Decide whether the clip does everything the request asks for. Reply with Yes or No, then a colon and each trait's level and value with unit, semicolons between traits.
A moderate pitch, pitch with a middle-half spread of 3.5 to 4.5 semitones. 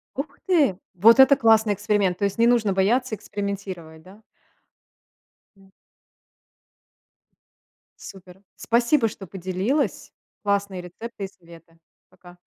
No: high, 200 Hz; average, 3.8 semitones